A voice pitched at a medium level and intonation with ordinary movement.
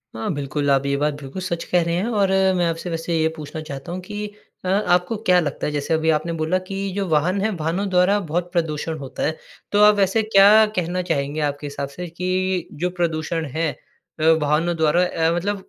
Yes: medium, 170 Hz; average, 3.3 semitones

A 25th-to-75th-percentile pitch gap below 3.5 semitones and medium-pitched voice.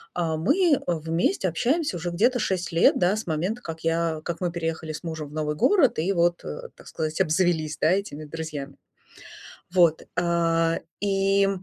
Yes: average, 3.1 semitones; medium, 170 Hz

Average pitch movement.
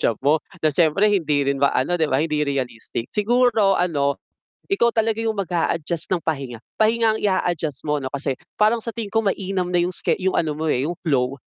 No: wide, 6.5 semitones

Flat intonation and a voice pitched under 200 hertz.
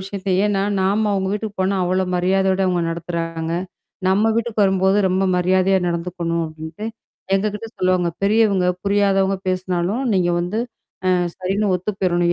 Yes: narrow, 1.9 semitones; high, 190 Hz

